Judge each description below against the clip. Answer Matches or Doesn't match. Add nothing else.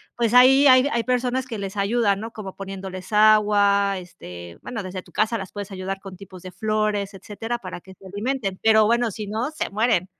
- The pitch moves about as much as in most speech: Matches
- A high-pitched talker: Matches